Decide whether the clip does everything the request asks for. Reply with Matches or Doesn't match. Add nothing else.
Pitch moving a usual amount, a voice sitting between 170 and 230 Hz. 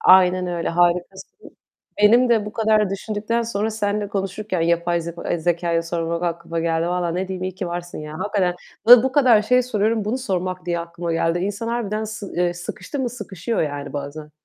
Matches